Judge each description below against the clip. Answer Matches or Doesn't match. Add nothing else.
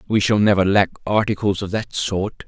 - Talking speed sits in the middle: Matches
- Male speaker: Matches